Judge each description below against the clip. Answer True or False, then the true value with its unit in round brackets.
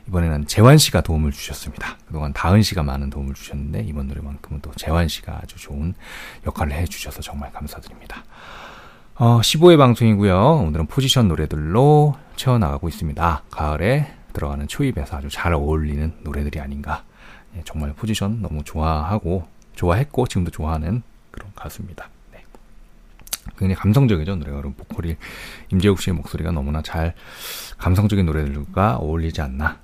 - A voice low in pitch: True (80 Hz)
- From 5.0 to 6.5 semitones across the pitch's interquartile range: True (5.5 semitones)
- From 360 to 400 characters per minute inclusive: True (370 characters per minute)